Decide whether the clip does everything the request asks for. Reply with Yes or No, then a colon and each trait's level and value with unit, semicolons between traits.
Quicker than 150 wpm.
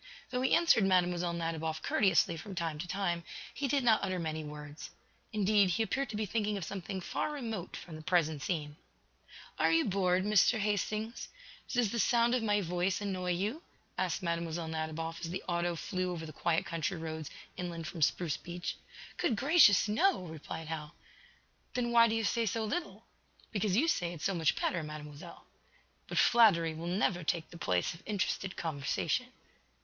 Yes: average, 180 wpm